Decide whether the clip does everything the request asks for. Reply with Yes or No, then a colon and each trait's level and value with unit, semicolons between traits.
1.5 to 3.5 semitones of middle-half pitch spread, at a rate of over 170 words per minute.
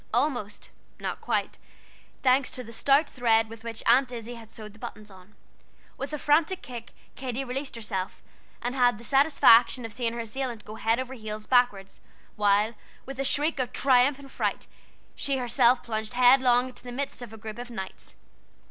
Yes: average, 2.8 semitones; average, 185 wpm